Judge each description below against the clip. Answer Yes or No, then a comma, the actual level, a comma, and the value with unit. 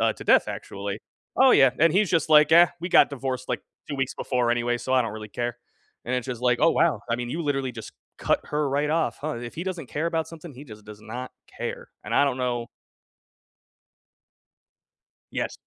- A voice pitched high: No, low, 130 Hz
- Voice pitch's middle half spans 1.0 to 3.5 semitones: No, average, 4.4 semitones